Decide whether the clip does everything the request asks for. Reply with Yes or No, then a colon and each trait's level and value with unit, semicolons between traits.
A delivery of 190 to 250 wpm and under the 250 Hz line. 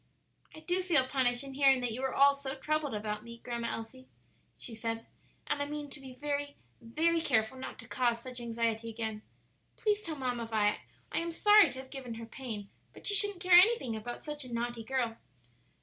No: fast, 205 wpm; very high, 260 Hz